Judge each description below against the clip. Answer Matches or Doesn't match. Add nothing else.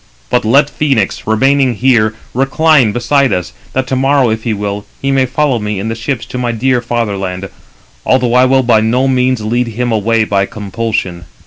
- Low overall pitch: Matches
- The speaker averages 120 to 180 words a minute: Doesn't match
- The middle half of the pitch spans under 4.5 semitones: Matches